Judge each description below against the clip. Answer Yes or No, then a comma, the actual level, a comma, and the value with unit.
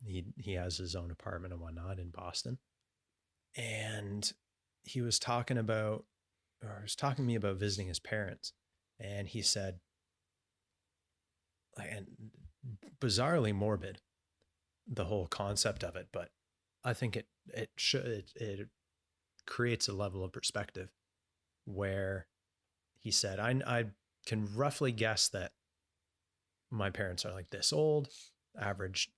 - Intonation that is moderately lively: Yes, average, 3.8 semitones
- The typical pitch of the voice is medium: No, low, 100 Hz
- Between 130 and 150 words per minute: Yes, slow, 135 wpm